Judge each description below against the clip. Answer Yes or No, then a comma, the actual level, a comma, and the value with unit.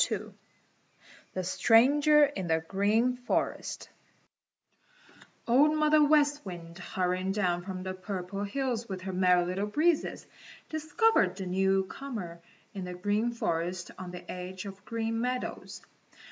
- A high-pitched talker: Yes, high, 195 Hz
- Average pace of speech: No, slow, 130 wpm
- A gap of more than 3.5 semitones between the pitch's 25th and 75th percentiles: Yes, wide, 5.6 semitones